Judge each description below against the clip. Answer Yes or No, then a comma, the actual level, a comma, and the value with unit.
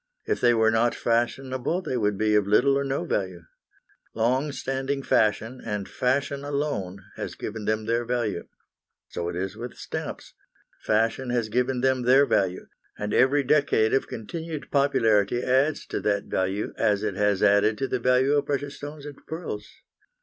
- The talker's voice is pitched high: No, low, 120 Hz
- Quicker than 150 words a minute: Yes, average, 170 wpm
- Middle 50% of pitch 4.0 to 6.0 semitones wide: Yes, average, 4.4 semitones